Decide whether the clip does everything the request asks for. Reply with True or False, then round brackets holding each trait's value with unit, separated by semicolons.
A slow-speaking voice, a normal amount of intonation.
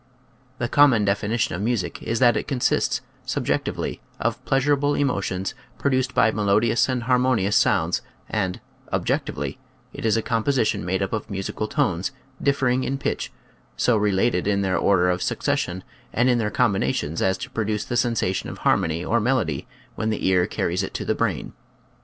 False (170 wpm; 4.7 semitones)